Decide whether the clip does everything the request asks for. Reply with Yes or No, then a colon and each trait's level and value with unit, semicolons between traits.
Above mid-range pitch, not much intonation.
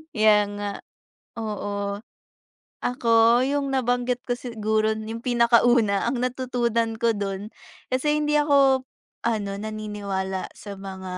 No: high, 230 Hz; average, 3.2 semitones